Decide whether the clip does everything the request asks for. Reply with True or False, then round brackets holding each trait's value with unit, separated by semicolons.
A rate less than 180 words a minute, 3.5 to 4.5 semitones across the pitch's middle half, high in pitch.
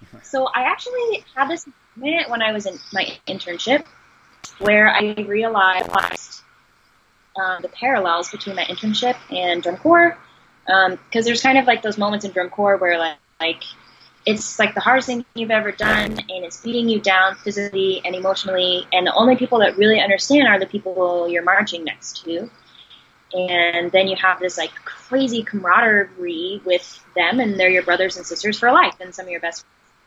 False (185 wpm; 4.2 semitones; 200 Hz)